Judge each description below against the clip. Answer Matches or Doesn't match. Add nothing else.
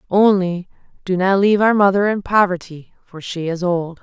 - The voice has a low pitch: Doesn't match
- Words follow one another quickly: Doesn't match